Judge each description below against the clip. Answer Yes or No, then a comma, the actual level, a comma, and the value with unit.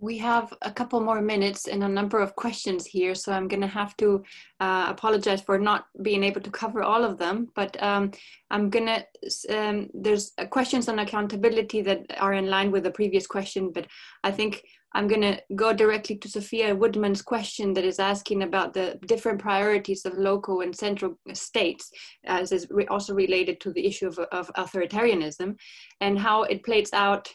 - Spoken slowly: No, average, 190 wpm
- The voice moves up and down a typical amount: No, narrow, 1.8 semitones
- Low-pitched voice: No, high, 200 Hz